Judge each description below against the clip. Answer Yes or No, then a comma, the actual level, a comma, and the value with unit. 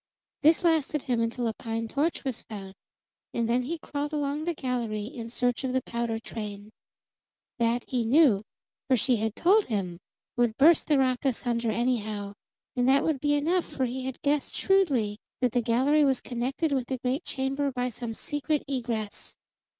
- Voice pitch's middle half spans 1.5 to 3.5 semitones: No, average, 3.9 semitones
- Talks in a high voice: Yes, very high, 250 Hz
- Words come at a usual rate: Yes, average, 180 wpm